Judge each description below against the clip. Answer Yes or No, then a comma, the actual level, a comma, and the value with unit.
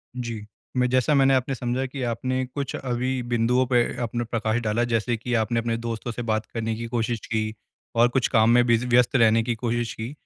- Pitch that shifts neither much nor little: No, narrow, 1.6 semitones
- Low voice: Yes, low, 120 Hz